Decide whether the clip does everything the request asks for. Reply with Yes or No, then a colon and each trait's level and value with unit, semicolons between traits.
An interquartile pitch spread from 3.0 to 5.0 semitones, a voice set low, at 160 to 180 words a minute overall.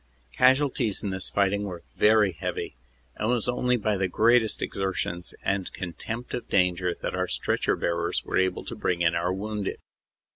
Yes: average, 3.6 semitones; low, 100 Hz; average, 175 wpm